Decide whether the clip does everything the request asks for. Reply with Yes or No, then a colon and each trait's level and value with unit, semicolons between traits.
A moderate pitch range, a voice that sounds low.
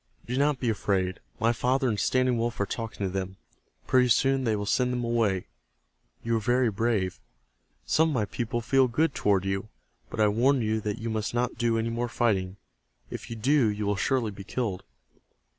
Yes: average, 3.4 semitones; low, 115 Hz